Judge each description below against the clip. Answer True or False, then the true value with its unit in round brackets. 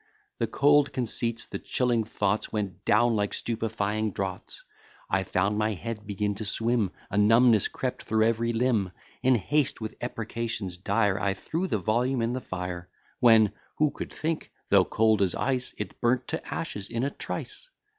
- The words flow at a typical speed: True (170 wpm)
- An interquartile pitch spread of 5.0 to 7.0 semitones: False (3.0 semitones)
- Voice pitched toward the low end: True (110 Hz)